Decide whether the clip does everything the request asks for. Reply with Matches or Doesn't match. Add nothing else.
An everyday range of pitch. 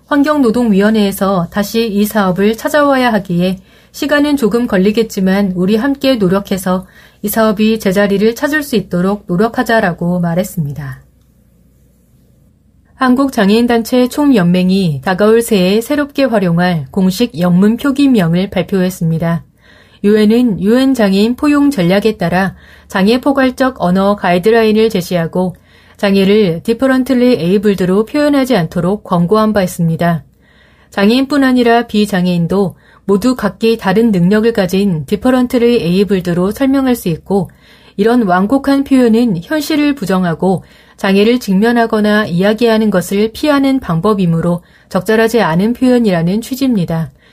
Matches